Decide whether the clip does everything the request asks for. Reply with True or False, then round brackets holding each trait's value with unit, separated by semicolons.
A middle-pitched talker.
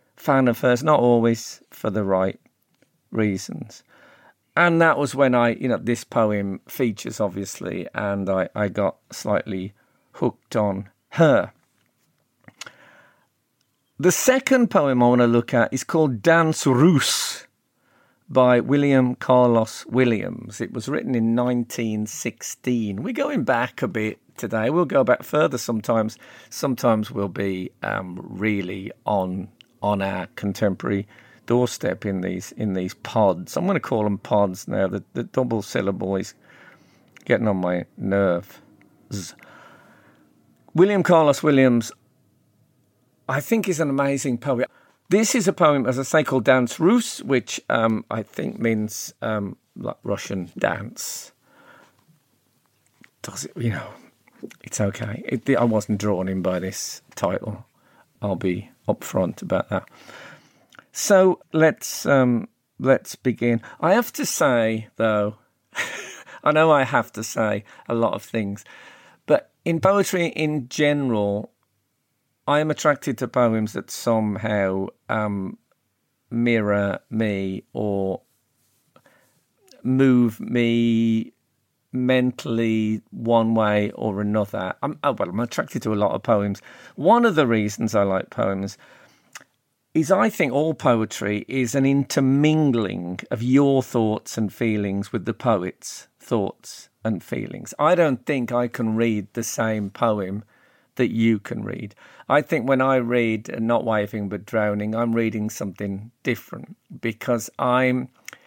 False (115 Hz)